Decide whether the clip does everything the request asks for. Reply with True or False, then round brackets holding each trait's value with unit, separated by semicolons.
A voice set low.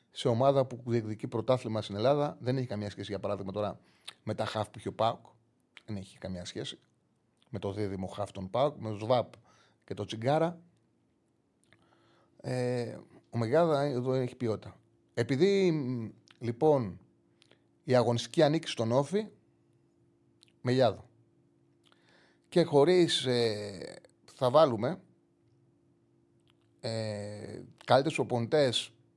True (120 Hz)